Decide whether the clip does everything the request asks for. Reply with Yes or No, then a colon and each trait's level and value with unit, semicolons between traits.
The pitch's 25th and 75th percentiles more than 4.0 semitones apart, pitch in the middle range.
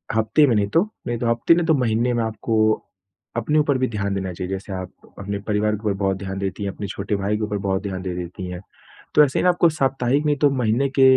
No: average, 4.8 semitones; low, 110 Hz